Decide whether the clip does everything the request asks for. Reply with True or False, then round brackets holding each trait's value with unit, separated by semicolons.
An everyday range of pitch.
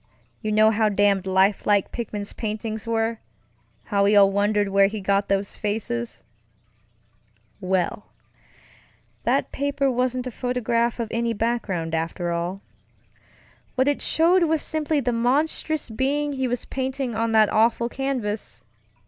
True (4.0 semitones)